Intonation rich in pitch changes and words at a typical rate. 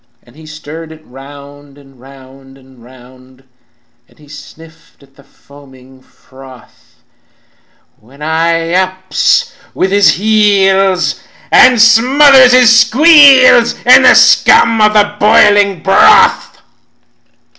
No: wide, 7.6 semitones; slow, 115 wpm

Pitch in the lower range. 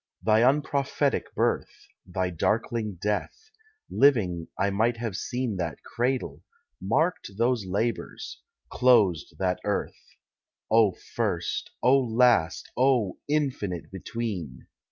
Yes: low, 110 Hz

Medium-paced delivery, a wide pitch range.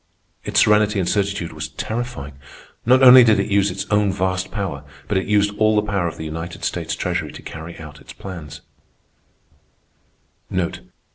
No: average, 165 wpm; average, 4.1 semitones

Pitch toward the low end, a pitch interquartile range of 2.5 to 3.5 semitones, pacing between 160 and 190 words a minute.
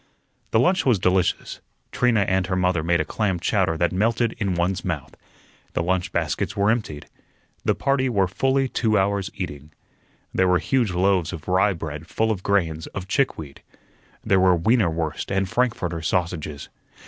No: very low, 95 Hz; average, 4.0 semitones; average, 170 wpm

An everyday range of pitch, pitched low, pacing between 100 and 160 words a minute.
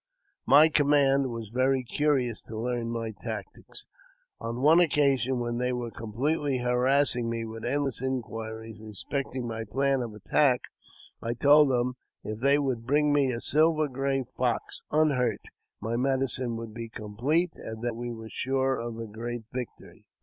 Yes: average, 3.1 semitones; low, 125 Hz; average, 155 wpm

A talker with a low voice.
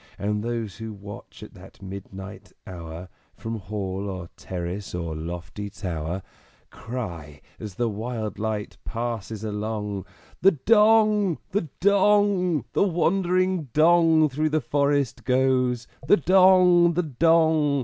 Yes: low, 120 Hz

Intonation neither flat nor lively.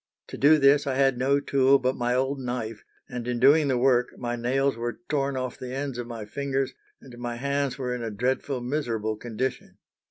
No: narrow, 2.3 semitones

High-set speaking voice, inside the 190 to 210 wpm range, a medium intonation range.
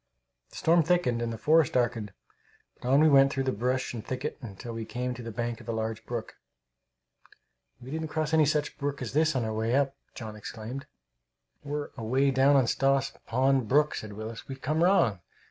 No: low, 130 Hz; average, 195 wpm; average, 3.8 semitones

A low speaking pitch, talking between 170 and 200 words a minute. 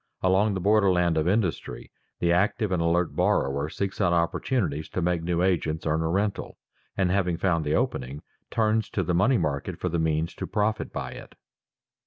Yes: very low, 90 Hz; average, 190 wpm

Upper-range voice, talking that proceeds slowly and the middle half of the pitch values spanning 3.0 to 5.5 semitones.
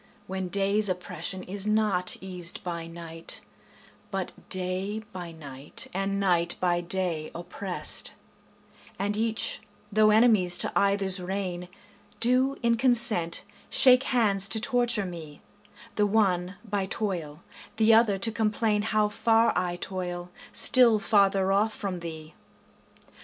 Yes: high, 195 Hz; slow, 125 wpm; average, 3.4 semitones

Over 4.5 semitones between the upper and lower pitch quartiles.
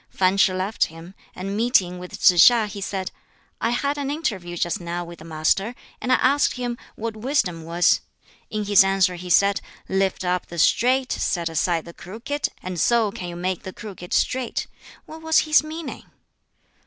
Yes: wide, 5.4 semitones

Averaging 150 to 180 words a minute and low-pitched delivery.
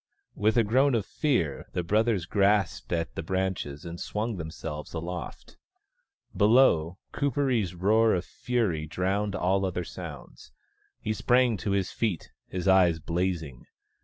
No: slow, 135 wpm; very low, 95 Hz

